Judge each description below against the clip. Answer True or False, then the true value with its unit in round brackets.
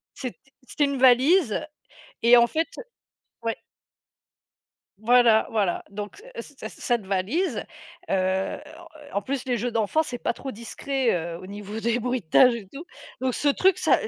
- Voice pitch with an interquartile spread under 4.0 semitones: False (4.5 semitones)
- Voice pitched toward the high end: True (235 Hz)